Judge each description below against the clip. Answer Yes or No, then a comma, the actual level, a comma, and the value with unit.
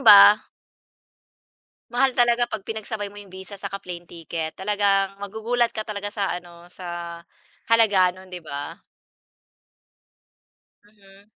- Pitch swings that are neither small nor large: Yes, average, 3.1 semitones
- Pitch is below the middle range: No, high, 200 Hz